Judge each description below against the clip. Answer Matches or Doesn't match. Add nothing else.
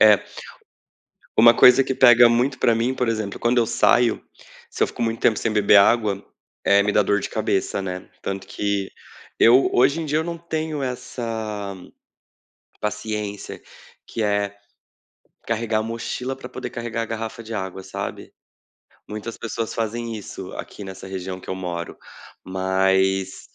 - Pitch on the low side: Matches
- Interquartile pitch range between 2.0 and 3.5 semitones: Matches